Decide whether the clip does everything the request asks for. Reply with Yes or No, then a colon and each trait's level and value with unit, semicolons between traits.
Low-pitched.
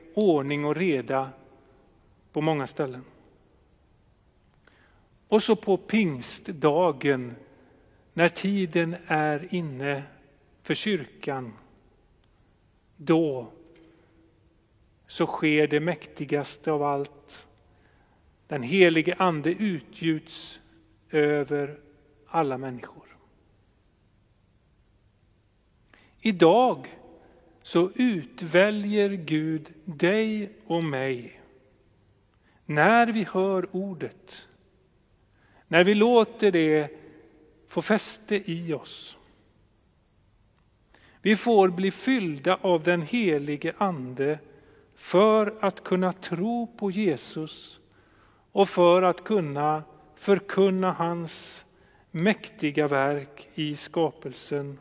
No: medium, 155 Hz